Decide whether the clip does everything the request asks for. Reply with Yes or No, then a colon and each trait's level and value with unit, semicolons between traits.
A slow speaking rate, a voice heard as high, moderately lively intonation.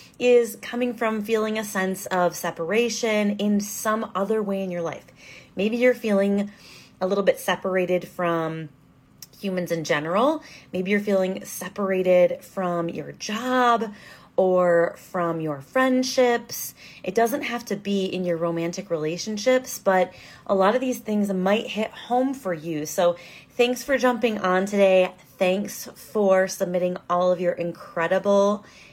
No: average, 145 wpm; high, 195 Hz; average, 3.6 semitones